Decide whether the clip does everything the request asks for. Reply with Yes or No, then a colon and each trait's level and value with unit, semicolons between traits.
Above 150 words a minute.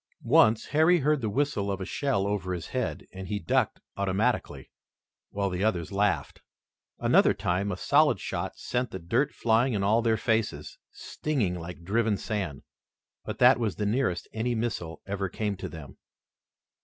Yes: average, 165 wpm